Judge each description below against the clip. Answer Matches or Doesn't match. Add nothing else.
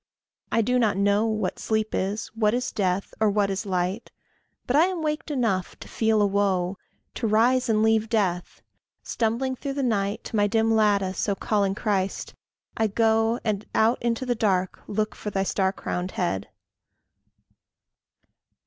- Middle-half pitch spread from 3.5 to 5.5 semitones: Doesn't match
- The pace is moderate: Matches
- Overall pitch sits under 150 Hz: Doesn't match